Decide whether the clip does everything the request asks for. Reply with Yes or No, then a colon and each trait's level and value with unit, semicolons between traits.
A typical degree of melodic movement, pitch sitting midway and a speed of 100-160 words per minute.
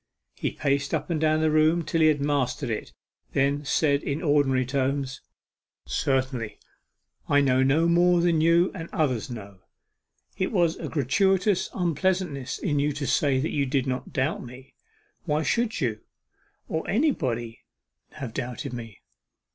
Yes: average, 4.1 semitones; medium, 145 Hz; average, 150 wpm